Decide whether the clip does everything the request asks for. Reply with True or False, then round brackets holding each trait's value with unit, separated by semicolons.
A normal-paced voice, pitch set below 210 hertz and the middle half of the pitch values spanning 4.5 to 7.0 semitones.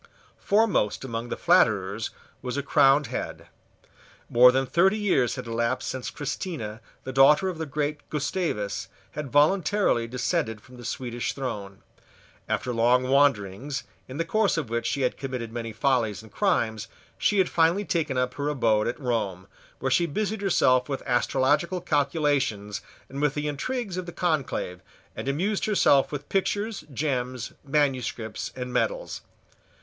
True (155 wpm; 135 Hz; 5.2 semitones)